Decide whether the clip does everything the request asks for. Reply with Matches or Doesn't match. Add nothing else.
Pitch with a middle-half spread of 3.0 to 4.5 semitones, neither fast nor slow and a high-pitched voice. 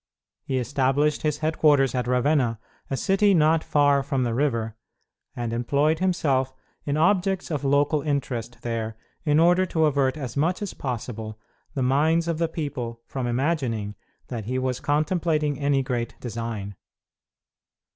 Doesn't match